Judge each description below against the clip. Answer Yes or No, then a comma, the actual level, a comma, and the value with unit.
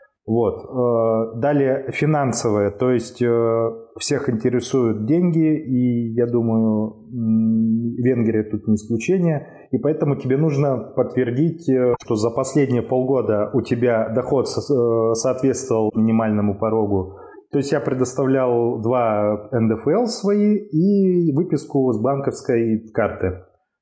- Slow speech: Yes, slow, 105 wpm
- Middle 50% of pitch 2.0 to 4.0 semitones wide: Yes, average, 3.6 semitones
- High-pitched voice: No, low, 120 Hz